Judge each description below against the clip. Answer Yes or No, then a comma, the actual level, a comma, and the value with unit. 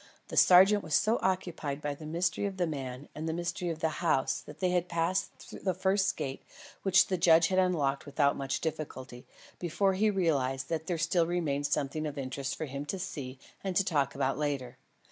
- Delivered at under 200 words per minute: No, fast, 205 wpm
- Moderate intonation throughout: Yes, average, 4.4 semitones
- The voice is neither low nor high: Yes, medium, 160 Hz